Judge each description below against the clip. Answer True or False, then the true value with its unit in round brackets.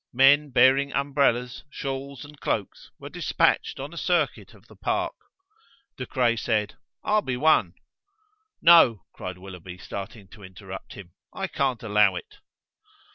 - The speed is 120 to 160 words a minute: True (140 wpm)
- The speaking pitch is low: True (125 Hz)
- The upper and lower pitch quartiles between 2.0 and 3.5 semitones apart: False (5.6 semitones)